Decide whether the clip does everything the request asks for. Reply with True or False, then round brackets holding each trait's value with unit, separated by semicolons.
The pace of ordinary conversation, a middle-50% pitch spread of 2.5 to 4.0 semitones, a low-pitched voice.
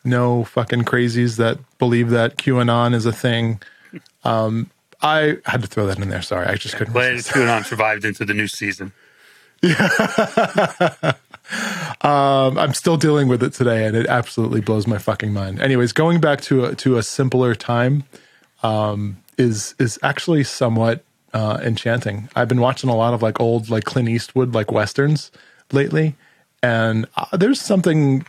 True (165 wpm; 3.4 semitones; 120 Hz)